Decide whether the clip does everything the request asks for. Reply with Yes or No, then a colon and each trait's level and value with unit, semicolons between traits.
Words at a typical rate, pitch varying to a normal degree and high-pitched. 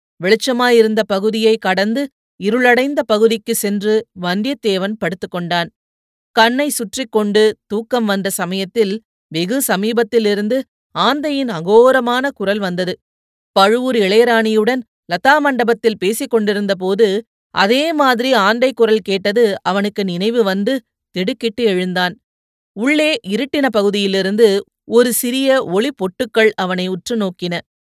Yes: average, 95 wpm; average, 3.8 semitones; high, 220 Hz